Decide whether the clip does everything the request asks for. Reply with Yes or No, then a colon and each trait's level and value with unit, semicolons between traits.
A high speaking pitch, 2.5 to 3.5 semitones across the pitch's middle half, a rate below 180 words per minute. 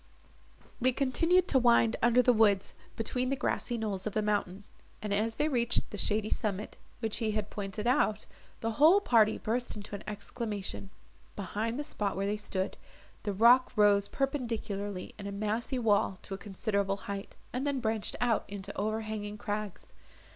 Yes: high, 215 Hz; average, 2.8 semitones; average, 170 wpm